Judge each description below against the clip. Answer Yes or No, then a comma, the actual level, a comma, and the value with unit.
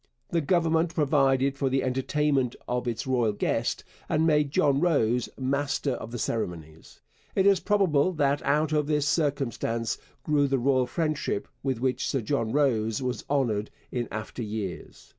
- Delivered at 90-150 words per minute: No, average, 160 wpm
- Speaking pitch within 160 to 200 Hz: No, low, 135 Hz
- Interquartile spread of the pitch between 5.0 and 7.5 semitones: No, average, 3.8 semitones